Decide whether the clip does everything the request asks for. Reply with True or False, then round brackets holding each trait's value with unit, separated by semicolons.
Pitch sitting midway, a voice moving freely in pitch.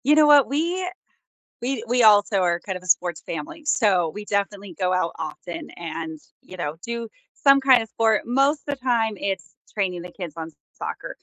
False (205 Hz; 6.5 semitones)